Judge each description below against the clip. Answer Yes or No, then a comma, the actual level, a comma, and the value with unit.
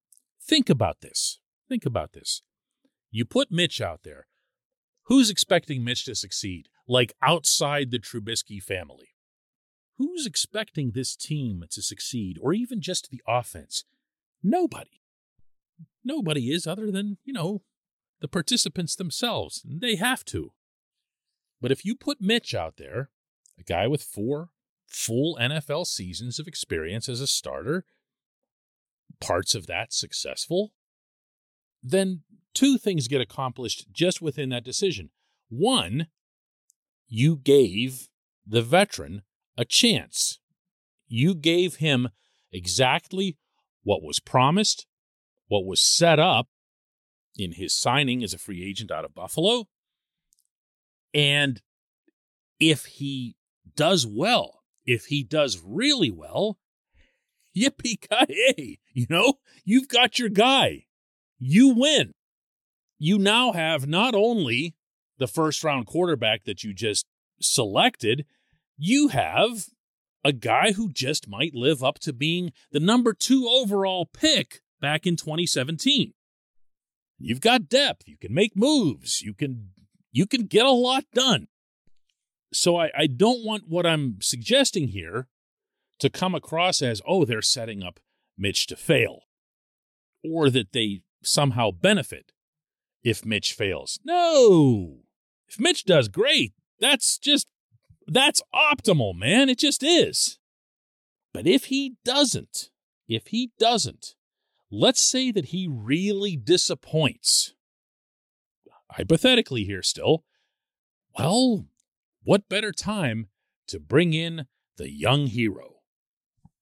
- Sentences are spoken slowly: Yes, slow, 120 wpm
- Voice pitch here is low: No, medium, 160 Hz